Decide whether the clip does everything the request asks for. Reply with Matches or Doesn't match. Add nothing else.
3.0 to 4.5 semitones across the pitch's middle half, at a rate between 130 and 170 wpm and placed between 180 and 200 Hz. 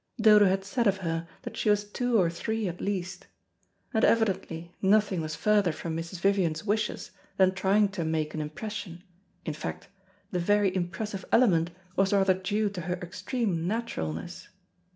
Matches